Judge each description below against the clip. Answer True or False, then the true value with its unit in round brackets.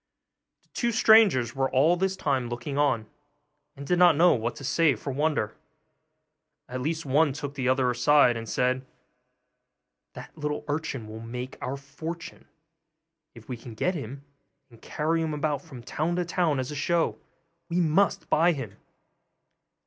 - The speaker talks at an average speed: True (165 wpm)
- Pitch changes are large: False (4.3 semitones)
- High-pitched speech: False (145 Hz)